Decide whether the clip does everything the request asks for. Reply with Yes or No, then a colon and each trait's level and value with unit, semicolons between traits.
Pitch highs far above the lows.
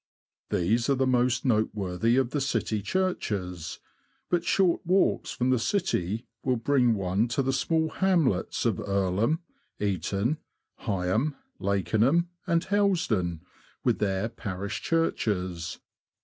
Yes: wide, 7.7 semitones